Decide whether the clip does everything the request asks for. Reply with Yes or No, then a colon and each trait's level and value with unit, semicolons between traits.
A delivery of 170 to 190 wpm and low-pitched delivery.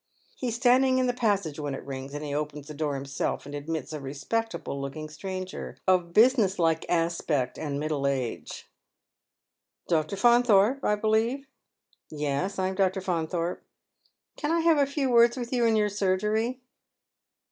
No: average, 180 wpm; medium, 185 Hz